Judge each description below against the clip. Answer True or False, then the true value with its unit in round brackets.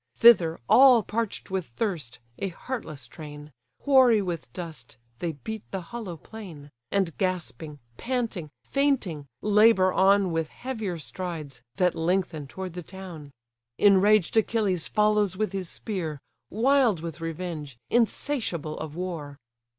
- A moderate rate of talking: False (125 wpm)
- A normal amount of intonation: True (5.0 semitones)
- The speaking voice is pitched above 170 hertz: True (185 Hz)